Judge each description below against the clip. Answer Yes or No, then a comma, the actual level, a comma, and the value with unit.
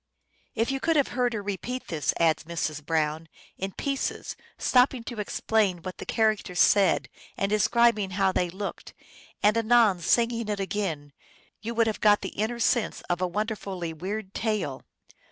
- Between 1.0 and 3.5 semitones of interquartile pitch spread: No, average, 4.2 semitones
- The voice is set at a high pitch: Yes, high, 205 Hz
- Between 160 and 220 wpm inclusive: Yes, average, 170 wpm